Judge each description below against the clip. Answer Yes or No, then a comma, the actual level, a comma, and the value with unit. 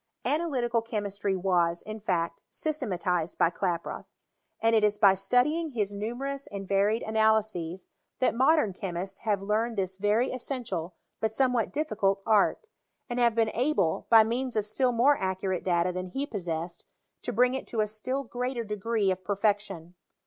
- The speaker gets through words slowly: No, average, 165 wpm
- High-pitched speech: Yes, high, 215 Hz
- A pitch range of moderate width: Yes, average, 4.3 semitones